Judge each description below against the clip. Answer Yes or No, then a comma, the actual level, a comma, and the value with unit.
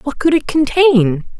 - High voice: Yes, very high, 270 Hz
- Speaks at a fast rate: No, average, 170 wpm